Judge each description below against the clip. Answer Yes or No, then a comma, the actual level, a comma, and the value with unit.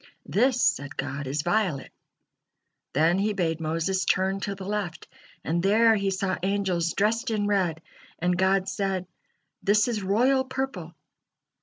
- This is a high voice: Yes, high, 195 Hz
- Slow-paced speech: No, average, 145 wpm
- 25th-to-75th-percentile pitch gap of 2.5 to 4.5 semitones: Yes, average, 3.4 semitones